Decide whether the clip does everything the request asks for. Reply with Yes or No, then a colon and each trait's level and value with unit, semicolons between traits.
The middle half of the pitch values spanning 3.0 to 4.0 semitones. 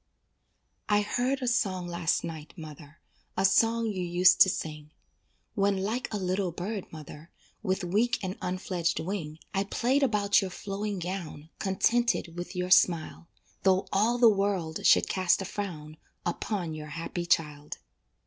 Yes: average, 3.4 semitones